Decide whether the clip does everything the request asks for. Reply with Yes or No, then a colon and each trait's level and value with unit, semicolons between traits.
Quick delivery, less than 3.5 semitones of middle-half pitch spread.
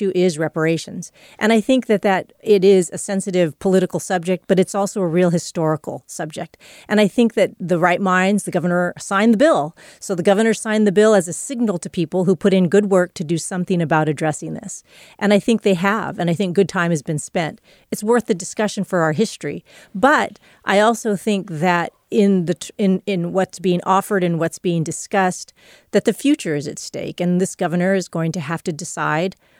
Yes: fast, 215 wpm; average, 2.7 semitones